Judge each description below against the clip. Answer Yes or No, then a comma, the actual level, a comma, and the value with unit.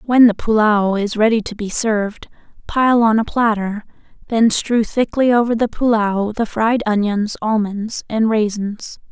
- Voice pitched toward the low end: No, high, 220 Hz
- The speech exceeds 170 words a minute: No, average, 160 wpm